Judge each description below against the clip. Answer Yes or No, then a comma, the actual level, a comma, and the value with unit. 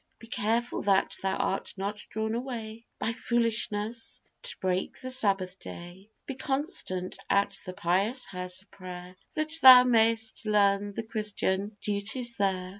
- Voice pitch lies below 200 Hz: No, high, 210 Hz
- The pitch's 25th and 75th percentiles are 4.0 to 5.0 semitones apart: No, average, 3.6 semitones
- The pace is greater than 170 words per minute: No, average, 145 wpm